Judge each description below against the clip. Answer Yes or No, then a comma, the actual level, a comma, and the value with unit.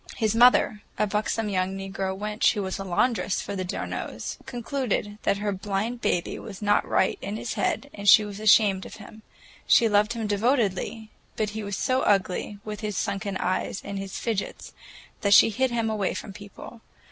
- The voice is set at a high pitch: Yes, high, 210 Hz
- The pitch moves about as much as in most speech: No, narrow, 2.1 semitones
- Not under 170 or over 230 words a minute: Yes, average, 185 wpm